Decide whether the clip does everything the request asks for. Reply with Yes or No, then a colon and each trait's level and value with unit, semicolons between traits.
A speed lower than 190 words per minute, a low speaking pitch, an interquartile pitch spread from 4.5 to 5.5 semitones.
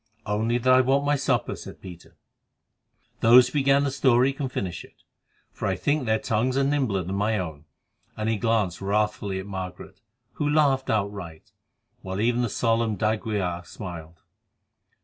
Yes: average, 165 wpm; low, 110 Hz; average, 5.1 semitones